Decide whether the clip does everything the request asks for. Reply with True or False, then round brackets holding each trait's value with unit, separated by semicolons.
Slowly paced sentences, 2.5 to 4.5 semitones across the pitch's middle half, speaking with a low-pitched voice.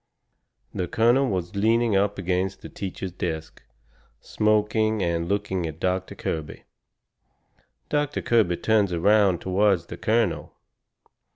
True (115 wpm; 3.3 semitones; 100 Hz)